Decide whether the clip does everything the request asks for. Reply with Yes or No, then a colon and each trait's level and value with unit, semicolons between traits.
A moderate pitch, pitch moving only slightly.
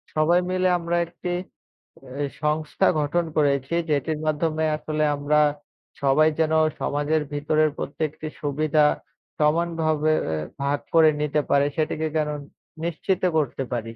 Yes: medium, 155 Hz; narrow, 1.4 semitones